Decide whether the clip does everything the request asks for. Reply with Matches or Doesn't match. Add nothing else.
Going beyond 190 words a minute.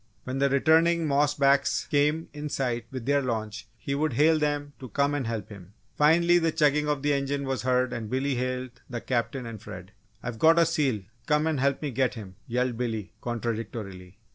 Matches